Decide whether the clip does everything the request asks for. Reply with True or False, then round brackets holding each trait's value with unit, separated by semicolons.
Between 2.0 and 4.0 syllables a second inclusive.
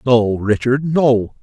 True (3.2 syllables/s)